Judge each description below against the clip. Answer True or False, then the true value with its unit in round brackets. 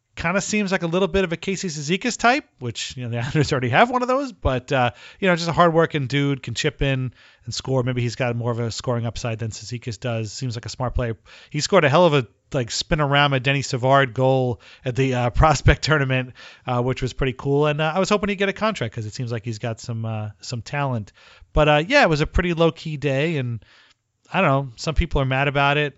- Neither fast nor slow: False (260 wpm)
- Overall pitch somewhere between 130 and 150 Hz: True (135 Hz)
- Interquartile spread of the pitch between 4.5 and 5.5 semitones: True (4.8 semitones)